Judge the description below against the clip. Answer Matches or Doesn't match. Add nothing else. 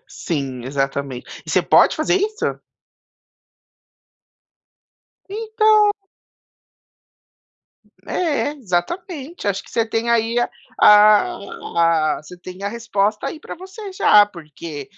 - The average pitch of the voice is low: Doesn't match